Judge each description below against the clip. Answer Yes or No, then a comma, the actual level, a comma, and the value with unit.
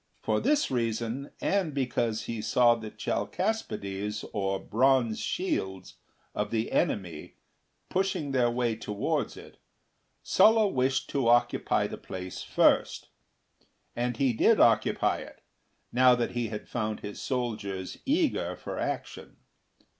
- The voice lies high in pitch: No, low, 120 Hz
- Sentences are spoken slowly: Yes, slow, 125 wpm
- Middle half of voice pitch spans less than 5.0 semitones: Yes, average, 4.0 semitones